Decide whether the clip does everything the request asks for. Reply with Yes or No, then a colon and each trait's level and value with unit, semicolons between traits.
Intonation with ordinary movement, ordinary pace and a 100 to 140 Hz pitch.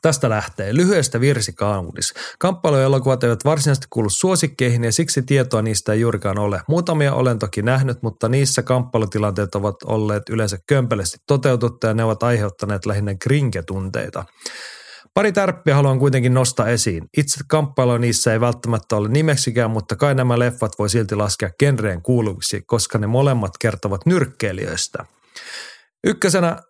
Yes: average, 4.7 semitones; average, 140 wpm; low, 120 Hz